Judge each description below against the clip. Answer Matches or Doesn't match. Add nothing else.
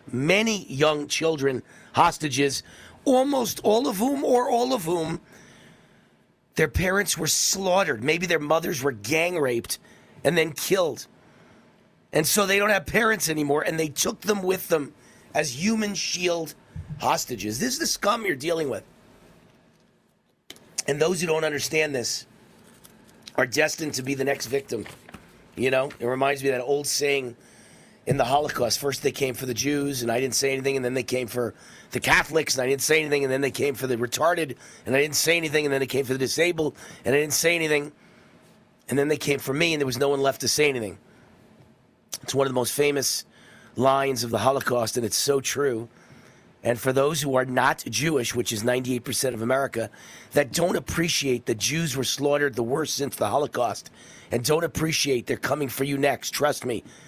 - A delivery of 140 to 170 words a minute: Doesn't match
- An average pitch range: Matches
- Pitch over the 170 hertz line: Doesn't match